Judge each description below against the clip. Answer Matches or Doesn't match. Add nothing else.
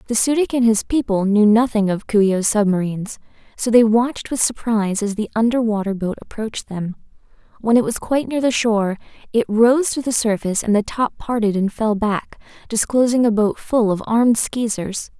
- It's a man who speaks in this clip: Doesn't match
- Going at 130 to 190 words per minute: Doesn't match